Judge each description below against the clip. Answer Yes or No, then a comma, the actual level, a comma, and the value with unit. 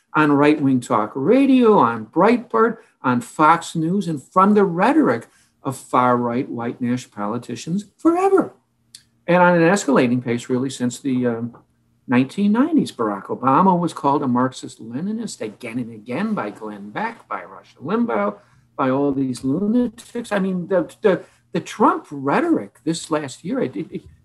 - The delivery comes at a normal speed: Yes, average, 150 wpm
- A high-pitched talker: No, medium, 140 Hz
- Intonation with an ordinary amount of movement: No, wide, 8.5 semitones